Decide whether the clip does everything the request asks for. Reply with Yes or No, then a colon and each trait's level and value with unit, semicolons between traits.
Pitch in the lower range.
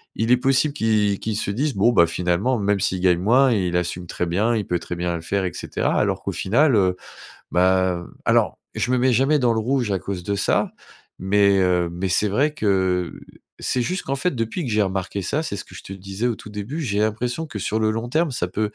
Yes: low, 105 Hz